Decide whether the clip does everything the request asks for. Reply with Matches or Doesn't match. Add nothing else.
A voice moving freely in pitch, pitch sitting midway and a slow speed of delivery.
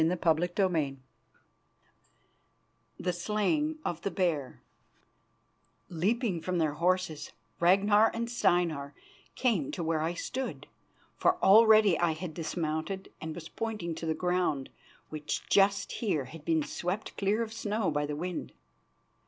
Doesn't match